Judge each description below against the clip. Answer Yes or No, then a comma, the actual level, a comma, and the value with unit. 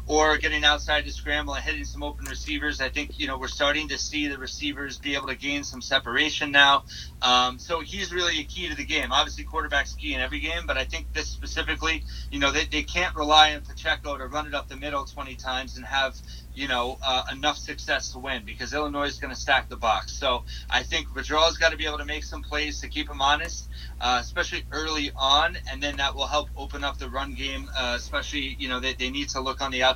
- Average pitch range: Yes, average, 3.1 semitones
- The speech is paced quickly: Yes, fast, 245 wpm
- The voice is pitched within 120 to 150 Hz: Yes, medium, 140 Hz